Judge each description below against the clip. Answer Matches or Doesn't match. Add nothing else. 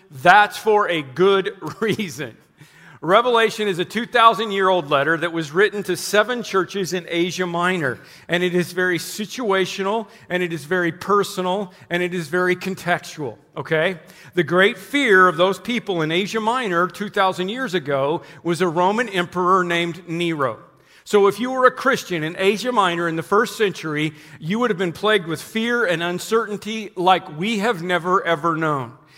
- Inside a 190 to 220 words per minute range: Doesn't match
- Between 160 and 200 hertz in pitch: Matches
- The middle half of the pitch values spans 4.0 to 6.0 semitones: Doesn't match